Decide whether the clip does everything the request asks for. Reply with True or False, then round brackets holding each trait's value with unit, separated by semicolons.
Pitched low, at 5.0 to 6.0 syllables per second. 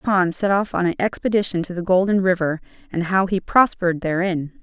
False (185 Hz; 5.4 syllables/s)